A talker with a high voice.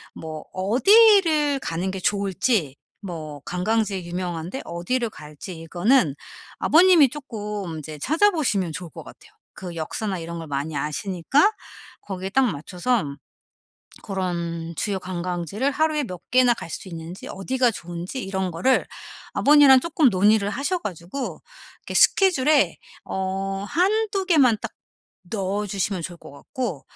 Yes: high, 195 Hz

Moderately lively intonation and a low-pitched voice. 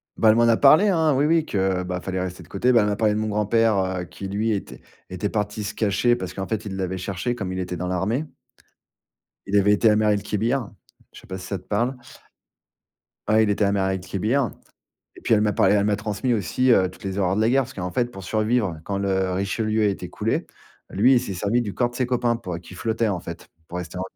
Yes: average, 3.4 semitones; low, 105 Hz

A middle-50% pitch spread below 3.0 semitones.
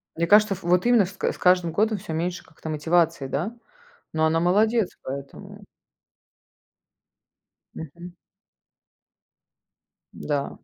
No: average, 3.7 semitones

